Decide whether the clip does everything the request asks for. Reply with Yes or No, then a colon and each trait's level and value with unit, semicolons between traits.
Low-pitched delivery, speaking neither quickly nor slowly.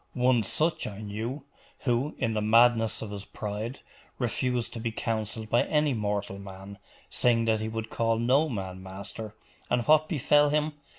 Yes: low, 115 Hz; average, 170 wpm